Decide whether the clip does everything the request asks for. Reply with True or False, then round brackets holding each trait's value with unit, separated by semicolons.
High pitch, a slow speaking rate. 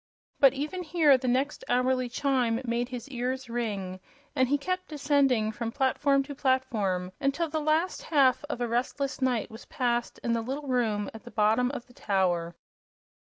False (255 Hz; 175 wpm)